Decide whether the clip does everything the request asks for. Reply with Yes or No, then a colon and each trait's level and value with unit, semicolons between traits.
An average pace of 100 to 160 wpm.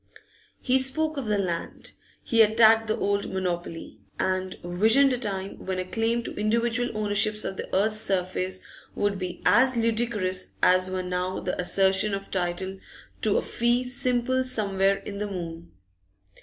Yes: average, 155 wpm